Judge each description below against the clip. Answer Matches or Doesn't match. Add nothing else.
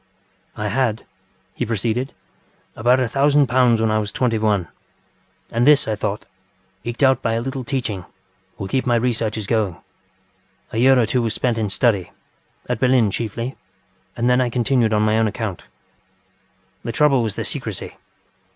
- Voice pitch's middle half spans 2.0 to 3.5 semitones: Matches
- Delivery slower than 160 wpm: Doesn't match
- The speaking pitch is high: Doesn't match